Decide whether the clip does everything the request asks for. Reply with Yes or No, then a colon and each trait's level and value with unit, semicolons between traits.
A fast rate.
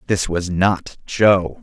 No: average, 150 wpm